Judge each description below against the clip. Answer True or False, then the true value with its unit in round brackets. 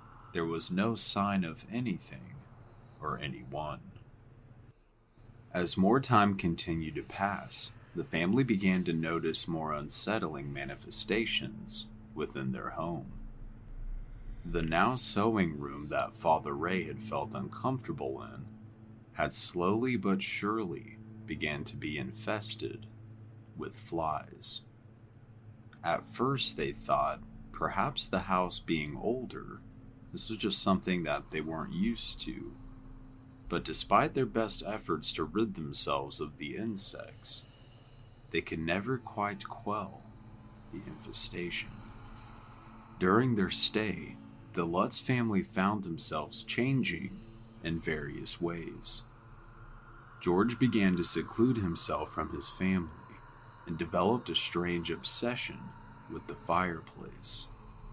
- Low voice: True (110 Hz)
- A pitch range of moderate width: True (3.7 semitones)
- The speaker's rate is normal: False (115 wpm)